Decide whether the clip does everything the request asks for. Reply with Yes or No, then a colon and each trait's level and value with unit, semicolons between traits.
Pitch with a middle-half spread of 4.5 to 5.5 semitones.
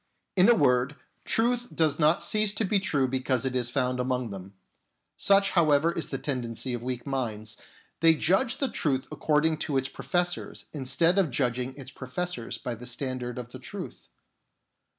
Yes: average, 5.1 semitones